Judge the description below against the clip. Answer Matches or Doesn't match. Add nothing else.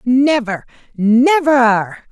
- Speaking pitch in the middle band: Doesn't match